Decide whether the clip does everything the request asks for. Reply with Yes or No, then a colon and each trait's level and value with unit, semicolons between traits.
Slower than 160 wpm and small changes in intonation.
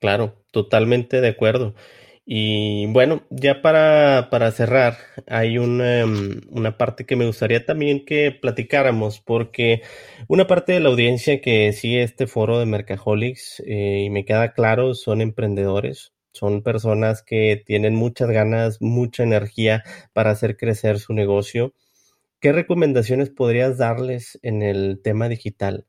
No: average, 140 wpm; average, 3.0 semitones